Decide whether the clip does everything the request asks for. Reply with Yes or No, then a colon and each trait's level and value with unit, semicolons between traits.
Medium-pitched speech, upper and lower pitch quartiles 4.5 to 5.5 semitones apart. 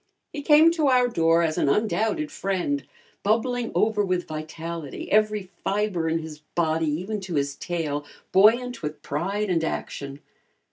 Yes: medium, 180 Hz; average, 5.2 semitones